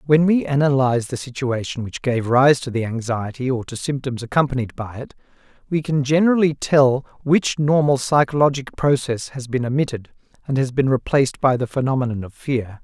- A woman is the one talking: No, male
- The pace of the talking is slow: No, average, 175 wpm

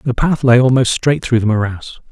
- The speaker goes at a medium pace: No, fast, 225 wpm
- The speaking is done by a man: Yes, male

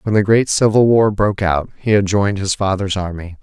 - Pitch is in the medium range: No, low, 100 Hz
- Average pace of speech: No, fast, 230 wpm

